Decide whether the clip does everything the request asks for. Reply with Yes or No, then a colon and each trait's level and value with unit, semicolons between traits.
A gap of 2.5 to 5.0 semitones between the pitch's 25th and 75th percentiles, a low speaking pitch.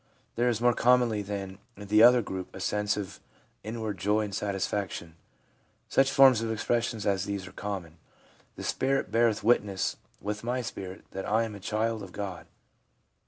Yes: average, 2.8 semitones; low, 105 Hz